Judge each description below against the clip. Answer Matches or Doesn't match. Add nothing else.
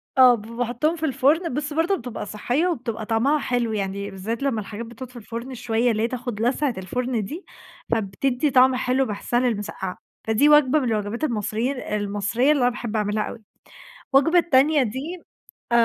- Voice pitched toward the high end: Matches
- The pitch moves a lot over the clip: Doesn't match